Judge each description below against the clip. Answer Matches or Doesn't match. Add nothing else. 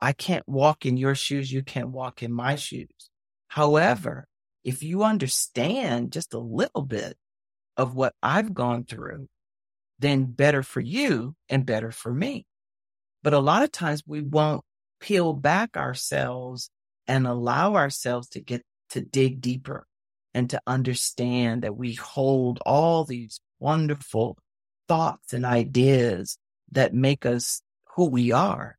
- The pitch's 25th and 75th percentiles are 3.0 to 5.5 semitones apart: Matches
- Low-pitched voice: Matches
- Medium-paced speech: Matches